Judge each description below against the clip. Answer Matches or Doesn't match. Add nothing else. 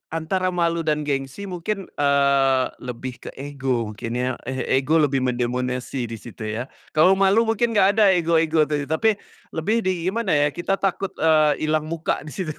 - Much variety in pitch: Matches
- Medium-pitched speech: Matches